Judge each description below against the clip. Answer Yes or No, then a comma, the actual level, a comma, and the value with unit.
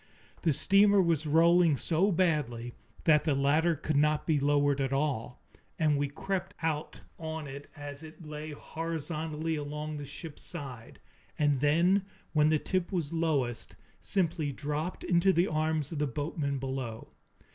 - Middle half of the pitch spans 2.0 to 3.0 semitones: Yes, narrow, 2.5 semitones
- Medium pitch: Yes, medium, 155 Hz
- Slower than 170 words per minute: Yes, average, 155 wpm